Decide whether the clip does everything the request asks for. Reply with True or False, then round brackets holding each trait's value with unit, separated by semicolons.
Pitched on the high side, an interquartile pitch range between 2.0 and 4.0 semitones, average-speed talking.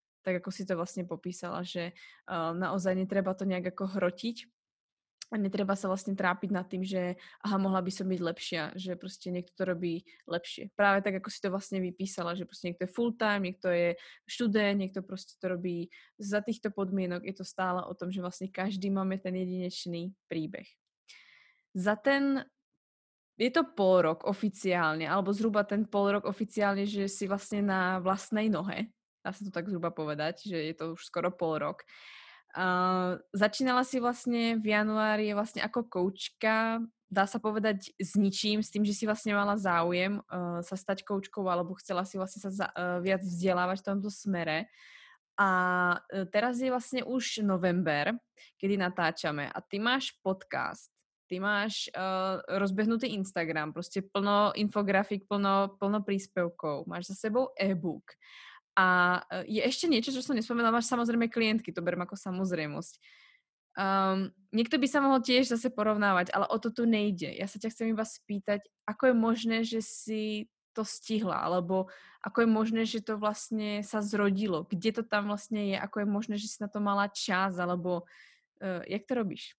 False (195 Hz; 2.9 semitones; 175 wpm)